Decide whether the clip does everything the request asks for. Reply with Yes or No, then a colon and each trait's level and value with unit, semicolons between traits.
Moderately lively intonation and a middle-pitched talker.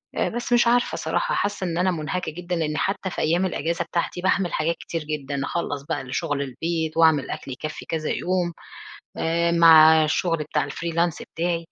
No: narrow, 2.3 semitones; medium, 165 Hz